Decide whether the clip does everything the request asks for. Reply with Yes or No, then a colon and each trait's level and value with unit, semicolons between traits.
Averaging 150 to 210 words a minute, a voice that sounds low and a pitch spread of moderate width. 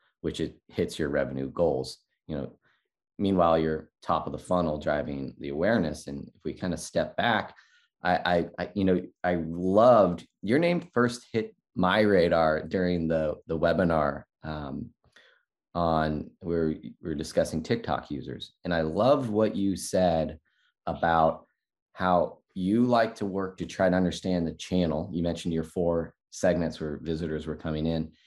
Yes: average, 165 wpm; very low, 85 Hz; average, 3.0 semitones